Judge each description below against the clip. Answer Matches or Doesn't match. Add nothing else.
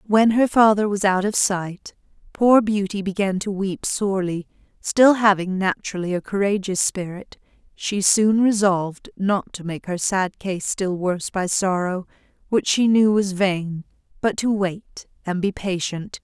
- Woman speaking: Matches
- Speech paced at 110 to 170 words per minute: Matches